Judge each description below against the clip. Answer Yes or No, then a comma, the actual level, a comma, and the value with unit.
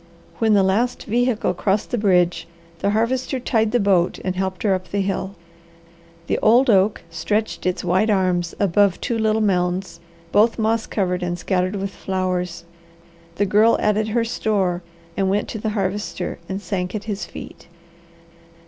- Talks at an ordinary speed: Yes, average, 165 wpm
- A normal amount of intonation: Yes, average, 3.0 semitones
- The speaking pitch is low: No, high, 200 Hz